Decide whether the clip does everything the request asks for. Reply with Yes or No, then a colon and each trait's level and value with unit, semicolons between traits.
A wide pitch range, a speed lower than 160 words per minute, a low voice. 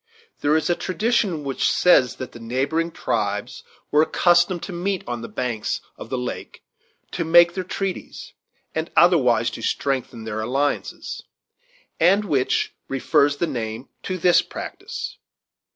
No: wide, 6.1 semitones; average, 145 wpm; medium, 155 Hz